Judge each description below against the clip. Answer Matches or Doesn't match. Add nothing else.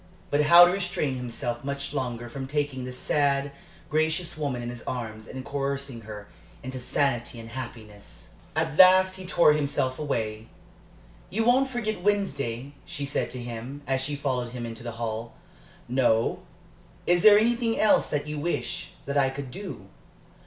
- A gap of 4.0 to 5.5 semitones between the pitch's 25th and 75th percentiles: Matches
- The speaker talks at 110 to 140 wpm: Doesn't match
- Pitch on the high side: Doesn't match